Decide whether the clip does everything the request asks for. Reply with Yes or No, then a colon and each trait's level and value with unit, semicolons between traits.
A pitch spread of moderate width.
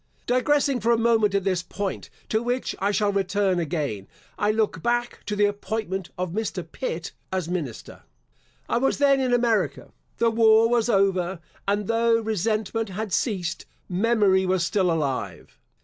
Yes: average, 3.6 semitones